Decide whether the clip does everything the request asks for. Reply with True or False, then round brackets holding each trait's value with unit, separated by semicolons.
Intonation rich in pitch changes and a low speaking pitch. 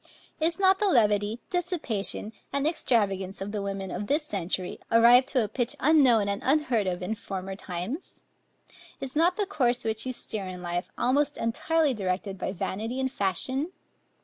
False (6.5 semitones; 230 Hz)